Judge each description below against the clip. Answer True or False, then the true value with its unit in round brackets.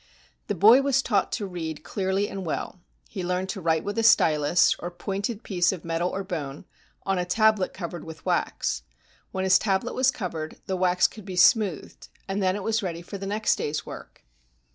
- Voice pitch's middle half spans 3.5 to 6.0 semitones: False (2.9 semitones)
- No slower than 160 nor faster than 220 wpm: True (200 wpm)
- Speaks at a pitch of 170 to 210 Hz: True (190 Hz)